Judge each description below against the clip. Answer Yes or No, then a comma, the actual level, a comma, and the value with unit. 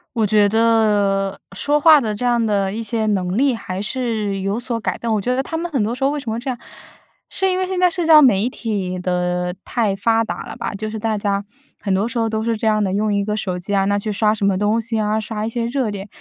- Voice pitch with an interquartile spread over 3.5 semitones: No, average, 2.9 semitones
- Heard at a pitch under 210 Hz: No, high, 215 Hz